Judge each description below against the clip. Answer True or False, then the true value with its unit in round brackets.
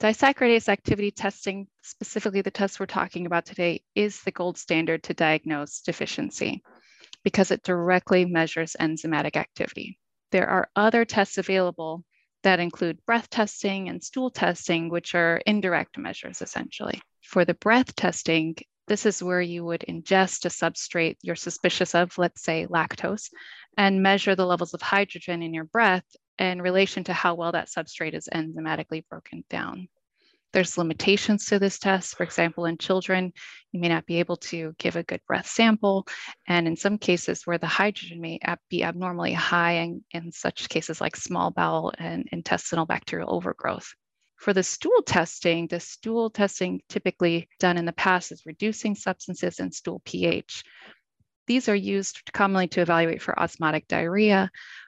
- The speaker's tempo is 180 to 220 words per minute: False (160 wpm)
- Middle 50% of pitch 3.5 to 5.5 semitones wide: False (2.8 semitones)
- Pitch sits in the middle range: True (180 Hz)